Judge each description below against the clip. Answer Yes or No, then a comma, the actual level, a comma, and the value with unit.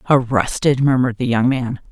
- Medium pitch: No, low, 125 Hz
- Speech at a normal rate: Yes, average, 155 wpm